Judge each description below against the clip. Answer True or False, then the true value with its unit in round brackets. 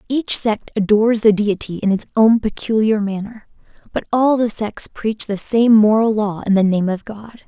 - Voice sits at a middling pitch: False (215 Hz)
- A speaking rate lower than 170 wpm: False (195 wpm)